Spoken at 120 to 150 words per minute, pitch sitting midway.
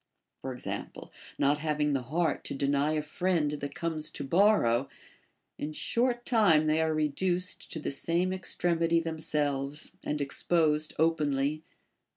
Yes: average, 140 wpm; medium, 155 Hz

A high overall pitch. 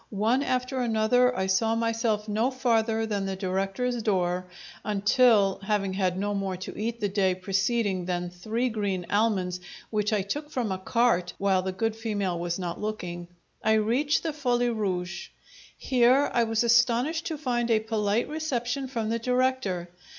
Yes: high, 215 Hz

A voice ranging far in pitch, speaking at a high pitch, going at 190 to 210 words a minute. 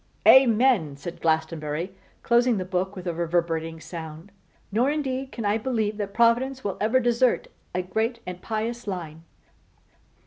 No: wide, 5.8 semitones; high, 205 Hz; average, 145 wpm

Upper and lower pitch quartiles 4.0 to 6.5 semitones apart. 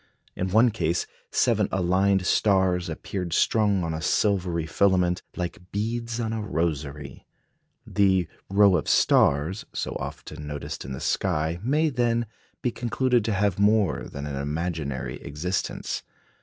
Yes: average, 4.7 semitones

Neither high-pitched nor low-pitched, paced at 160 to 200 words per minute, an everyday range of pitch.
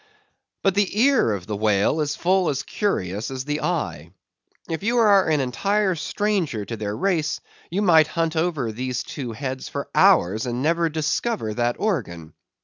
No: medium, 150 Hz; average, 170 wpm; wide, 8.5 semitones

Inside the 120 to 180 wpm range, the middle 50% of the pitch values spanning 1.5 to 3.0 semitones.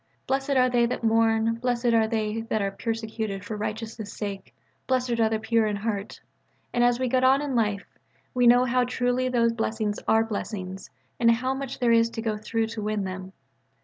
No: fast, 205 wpm; narrow, 2.4 semitones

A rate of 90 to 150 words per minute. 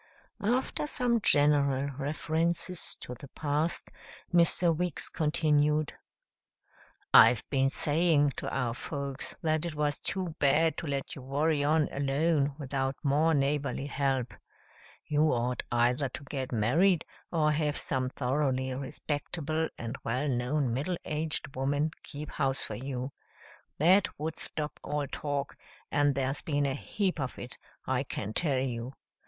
Yes: average, 140 wpm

